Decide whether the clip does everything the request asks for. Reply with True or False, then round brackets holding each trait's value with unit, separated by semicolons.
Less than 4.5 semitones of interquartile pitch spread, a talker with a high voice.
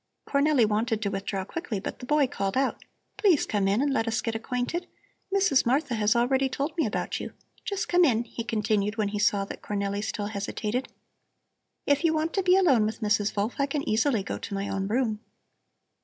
False (5.3 semitones; 230 Hz)